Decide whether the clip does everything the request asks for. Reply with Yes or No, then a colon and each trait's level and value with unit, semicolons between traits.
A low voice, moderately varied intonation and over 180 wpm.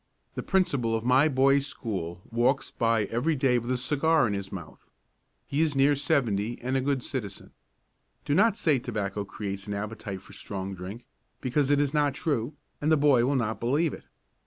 Yes: low, 125 Hz; average, 5.0 semitones; average, 190 wpm